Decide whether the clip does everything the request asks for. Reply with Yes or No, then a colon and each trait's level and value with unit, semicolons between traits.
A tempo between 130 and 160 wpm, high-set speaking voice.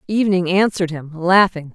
No: average, 140 wpm; medium, 180 Hz